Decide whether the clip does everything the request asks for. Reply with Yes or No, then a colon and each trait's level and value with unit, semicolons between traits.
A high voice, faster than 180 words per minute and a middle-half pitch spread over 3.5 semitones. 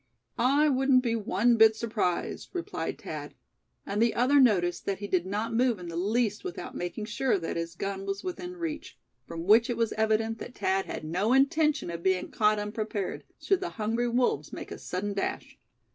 Yes: high, 220 Hz; average, 190 wpm; average, 4.3 semitones